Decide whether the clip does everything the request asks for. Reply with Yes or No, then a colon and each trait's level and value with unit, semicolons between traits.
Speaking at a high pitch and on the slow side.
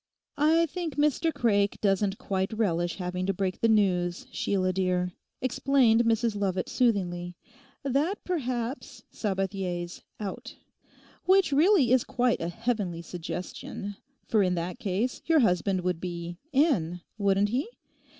Yes: high, 200 Hz; slow, 130 wpm